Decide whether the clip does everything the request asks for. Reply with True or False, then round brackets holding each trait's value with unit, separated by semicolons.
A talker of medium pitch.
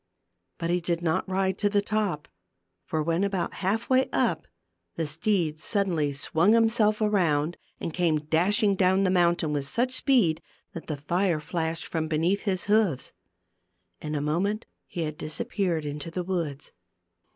True (175 Hz)